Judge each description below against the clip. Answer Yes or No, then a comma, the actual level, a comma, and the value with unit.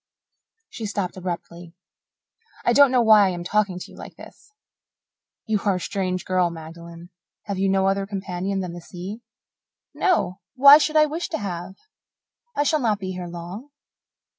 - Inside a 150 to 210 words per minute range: Yes, average, 170 wpm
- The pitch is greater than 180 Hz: Yes, high, 190 Hz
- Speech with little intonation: No, average, 3.5 semitones